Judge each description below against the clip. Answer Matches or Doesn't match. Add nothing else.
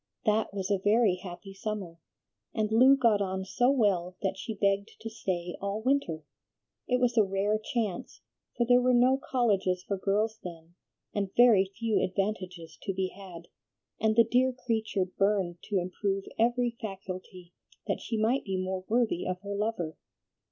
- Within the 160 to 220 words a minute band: Matches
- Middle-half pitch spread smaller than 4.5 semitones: Matches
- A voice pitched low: Doesn't match